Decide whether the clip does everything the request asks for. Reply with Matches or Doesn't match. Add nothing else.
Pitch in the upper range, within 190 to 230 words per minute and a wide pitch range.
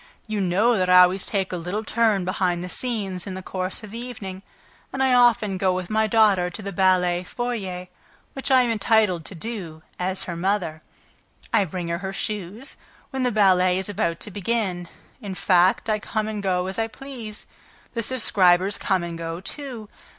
Doesn't match